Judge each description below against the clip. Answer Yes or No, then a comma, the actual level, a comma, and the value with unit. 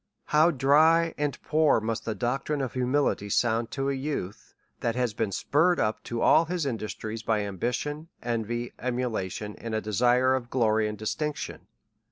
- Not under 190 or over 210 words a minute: No, average, 165 wpm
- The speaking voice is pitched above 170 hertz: No, low, 125 Hz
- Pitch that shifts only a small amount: No, average, 4.6 semitones